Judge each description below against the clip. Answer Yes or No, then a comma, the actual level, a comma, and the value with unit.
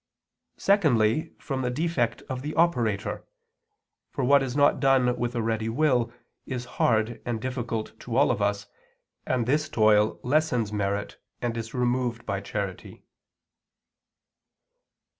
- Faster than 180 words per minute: No, slow, 135 wpm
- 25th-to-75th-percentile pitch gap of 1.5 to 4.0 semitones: Yes, average, 3.4 semitones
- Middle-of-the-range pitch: No, low, 120 Hz